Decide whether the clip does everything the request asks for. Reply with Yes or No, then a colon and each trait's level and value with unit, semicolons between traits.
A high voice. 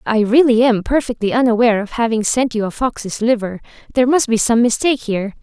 Yes: high, 230 Hz